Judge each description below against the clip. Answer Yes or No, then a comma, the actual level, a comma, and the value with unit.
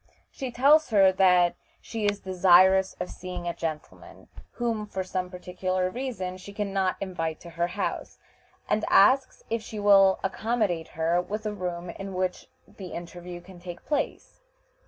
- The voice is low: No, medium, 185 Hz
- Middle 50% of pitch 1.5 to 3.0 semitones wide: Yes, average, 2.7 semitones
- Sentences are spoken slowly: No, average, 160 wpm